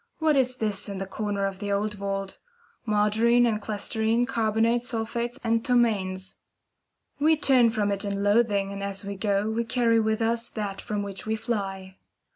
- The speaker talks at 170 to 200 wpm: Yes, average, 175 wpm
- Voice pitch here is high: Yes, high, 215 Hz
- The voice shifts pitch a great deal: No, average, 2.7 semitones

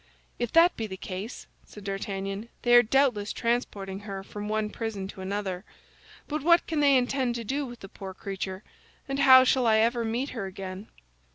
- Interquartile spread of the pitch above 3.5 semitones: Yes, average, 4.4 semitones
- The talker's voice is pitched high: Yes, high, 220 Hz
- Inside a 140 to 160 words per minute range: No, average, 190 wpm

